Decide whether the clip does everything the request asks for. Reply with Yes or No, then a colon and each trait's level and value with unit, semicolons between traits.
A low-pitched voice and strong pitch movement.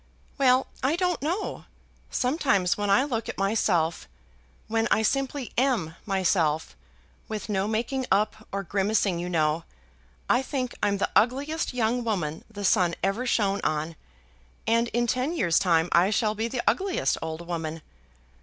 No: high, 215 Hz; wide, 6.0 semitones